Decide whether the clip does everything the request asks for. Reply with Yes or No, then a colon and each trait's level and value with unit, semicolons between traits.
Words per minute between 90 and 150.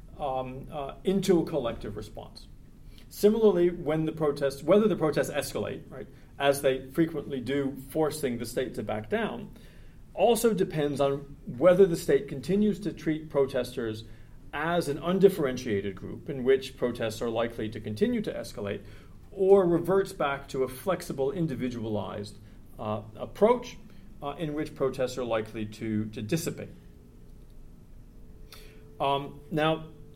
Yes: slow, 135 wpm